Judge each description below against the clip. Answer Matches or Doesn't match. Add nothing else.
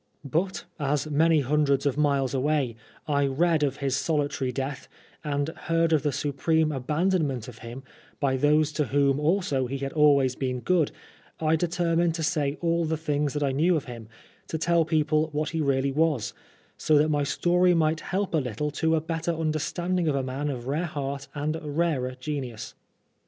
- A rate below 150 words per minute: Doesn't match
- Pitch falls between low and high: Matches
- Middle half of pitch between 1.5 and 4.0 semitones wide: Matches